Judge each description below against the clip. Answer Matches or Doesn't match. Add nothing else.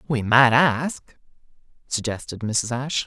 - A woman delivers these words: Doesn't match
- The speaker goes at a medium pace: Doesn't match